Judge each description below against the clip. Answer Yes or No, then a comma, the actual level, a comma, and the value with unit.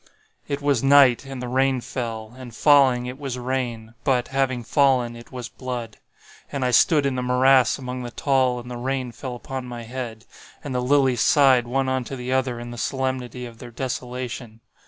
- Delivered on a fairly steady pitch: Yes, narrow, 1.6 semitones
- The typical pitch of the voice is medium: No, low, 125 Hz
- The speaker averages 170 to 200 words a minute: Yes, average, 190 wpm